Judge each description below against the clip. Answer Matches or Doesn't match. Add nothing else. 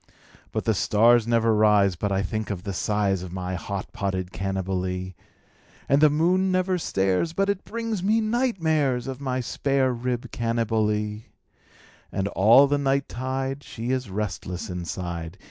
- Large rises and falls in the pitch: Matches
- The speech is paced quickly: Doesn't match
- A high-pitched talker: Doesn't match